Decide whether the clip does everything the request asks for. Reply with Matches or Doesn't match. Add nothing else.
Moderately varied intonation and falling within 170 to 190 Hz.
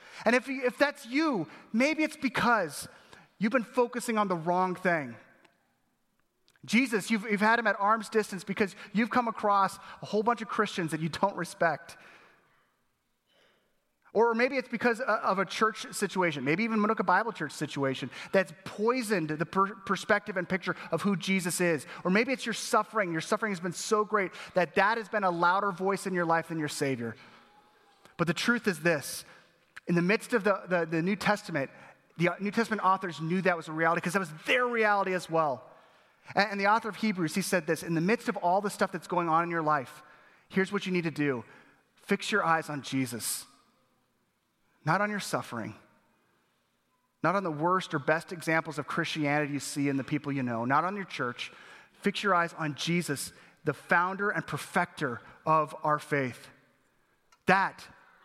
Matches